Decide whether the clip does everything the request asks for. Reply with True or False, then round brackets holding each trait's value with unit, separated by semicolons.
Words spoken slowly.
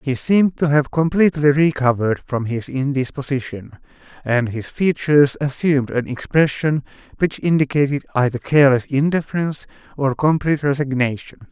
True (120 wpm)